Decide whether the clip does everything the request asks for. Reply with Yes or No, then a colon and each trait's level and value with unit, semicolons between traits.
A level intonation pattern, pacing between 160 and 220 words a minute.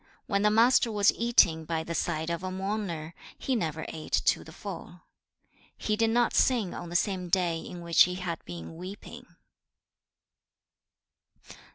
No: average, 4.1 semitones; average, 165 wpm